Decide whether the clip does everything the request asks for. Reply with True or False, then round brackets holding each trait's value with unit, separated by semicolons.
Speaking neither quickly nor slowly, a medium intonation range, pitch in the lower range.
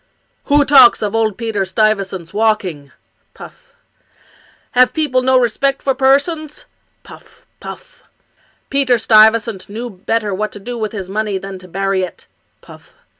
False (145 wpm; 4.7 semitones; 220 Hz)